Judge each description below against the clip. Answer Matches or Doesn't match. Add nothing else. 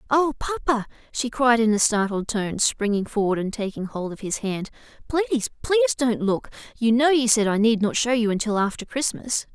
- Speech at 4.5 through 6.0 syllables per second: Matches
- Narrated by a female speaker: Matches